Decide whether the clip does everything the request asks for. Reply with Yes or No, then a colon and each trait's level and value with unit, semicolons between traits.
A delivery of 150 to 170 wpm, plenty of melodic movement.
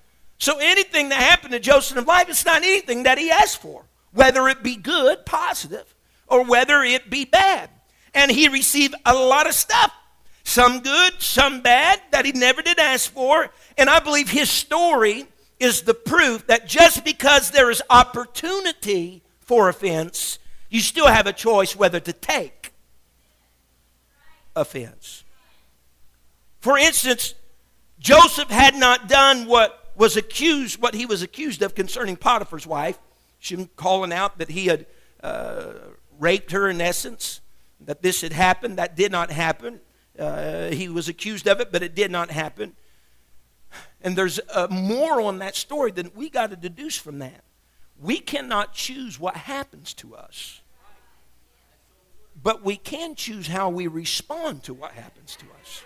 Yes: average, 160 wpm; wide, 8.4 semitones